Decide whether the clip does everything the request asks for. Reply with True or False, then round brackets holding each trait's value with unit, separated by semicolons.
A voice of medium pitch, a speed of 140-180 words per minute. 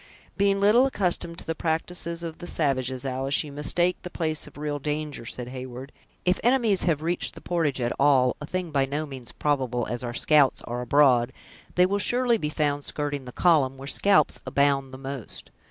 False (145 Hz; 195 wpm)